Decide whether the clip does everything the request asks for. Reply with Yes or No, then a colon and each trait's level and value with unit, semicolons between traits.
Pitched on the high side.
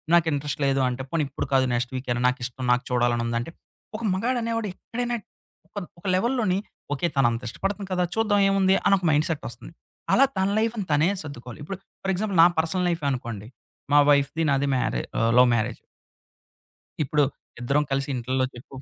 No: medium, 145 Hz